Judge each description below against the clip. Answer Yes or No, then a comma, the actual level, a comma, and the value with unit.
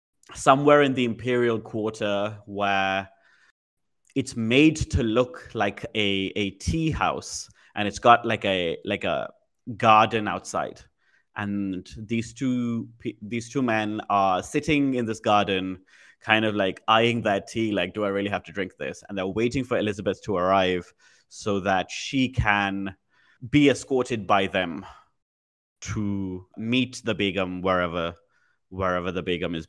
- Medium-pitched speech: No, low, 105 Hz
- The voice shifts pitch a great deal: No, average, 3.6 semitones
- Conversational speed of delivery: Yes, average, 150 wpm